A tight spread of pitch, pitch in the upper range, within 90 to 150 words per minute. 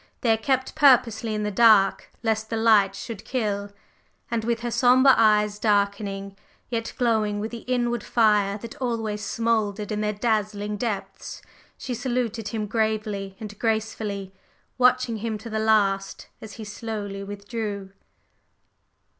Yes: narrow, 2.2 semitones; high, 220 Hz; average, 145 wpm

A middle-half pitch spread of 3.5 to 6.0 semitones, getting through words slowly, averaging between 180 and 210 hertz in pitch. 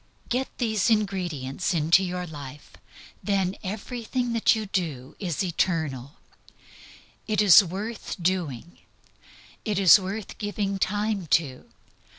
Yes: average, 4.2 semitones; slow, 115 wpm; high, 190 Hz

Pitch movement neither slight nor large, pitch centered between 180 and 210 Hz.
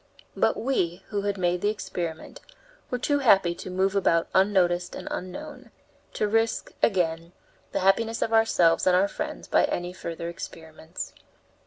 Yes: average, 3.3 semitones; medium, 185 Hz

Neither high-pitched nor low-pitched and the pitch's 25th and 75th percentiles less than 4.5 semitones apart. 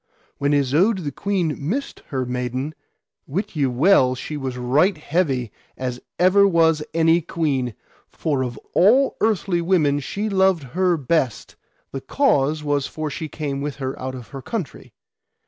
No: medium, 150 Hz; average, 5.2 semitones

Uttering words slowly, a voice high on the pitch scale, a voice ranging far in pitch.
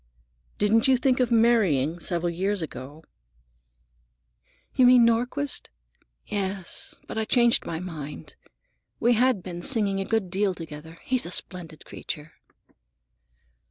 Yes: slow, 125 wpm; high, 195 Hz; wide, 5.9 semitones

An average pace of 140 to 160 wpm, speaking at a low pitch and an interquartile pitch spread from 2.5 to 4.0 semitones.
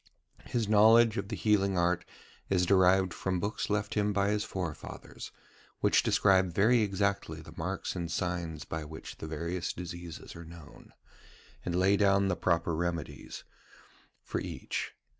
Yes: average, 150 wpm; very low, 95 Hz; average, 2.8 semitones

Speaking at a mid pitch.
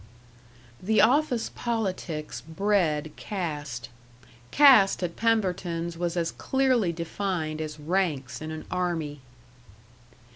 Yes: medium, 175 Hz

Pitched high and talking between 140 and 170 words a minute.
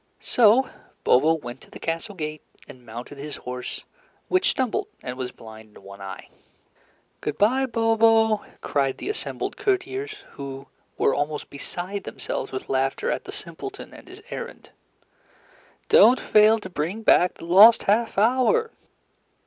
Yes: high, 195 Hz; average, 150 wpm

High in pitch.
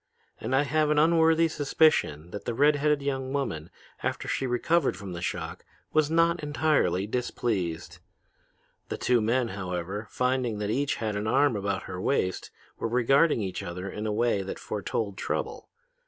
No: low, 120 Hz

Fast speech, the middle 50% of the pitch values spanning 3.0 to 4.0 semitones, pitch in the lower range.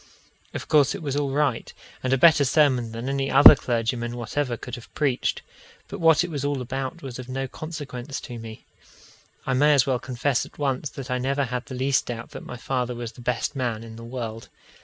No: fast, 220 wpm; narrow, 2.6 semitones; low, 130 Hz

